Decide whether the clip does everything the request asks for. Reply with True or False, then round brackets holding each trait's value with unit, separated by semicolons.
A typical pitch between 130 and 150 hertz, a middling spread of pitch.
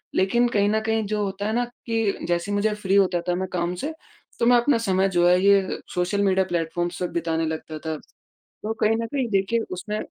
False (195 Hz; 3.6 semitones)